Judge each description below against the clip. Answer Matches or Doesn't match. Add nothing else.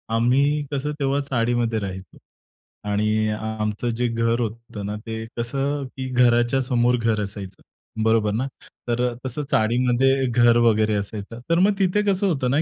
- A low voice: Matches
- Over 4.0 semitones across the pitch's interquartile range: Doesn't match